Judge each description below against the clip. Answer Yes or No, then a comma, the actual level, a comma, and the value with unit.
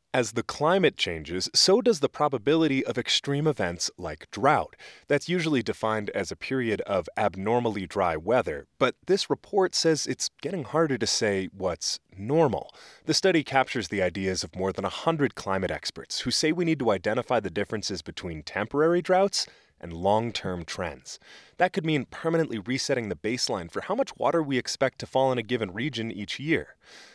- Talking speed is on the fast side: No, average, 180 wpm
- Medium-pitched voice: No, low, 125 Hz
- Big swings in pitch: Yes, wide, 7.5 semitones